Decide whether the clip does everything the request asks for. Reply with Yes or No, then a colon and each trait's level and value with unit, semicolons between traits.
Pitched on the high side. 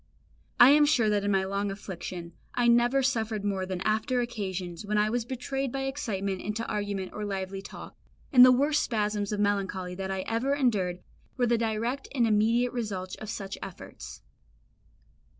Yes: high, 210 Hz